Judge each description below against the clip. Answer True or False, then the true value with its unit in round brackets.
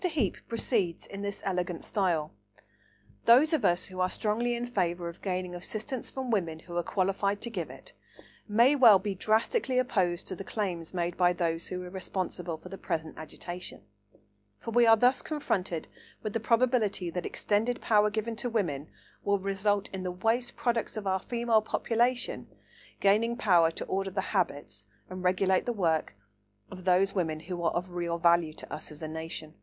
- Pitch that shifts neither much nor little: True (4.4 semitones)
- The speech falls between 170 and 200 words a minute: True (185 wpm)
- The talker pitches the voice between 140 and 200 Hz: True (190 Hz)